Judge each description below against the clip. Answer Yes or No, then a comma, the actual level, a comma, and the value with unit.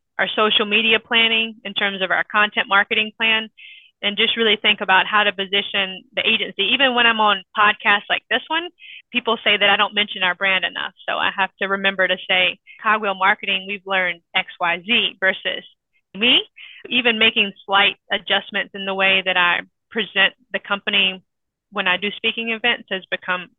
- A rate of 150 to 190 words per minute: Yes, average, 185 wpm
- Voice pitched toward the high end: Yes, high, 205 Hz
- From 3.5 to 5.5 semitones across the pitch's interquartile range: No, average, 2.7 semitones